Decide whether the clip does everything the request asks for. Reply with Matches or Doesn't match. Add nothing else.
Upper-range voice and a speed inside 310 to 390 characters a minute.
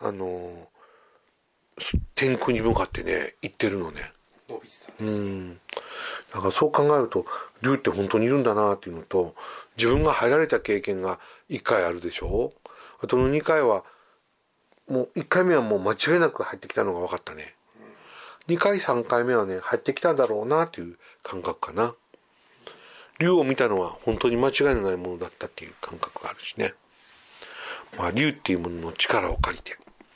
Doesn't match